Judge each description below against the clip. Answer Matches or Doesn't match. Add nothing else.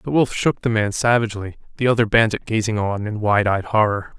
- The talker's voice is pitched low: Matches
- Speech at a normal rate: Doesn't match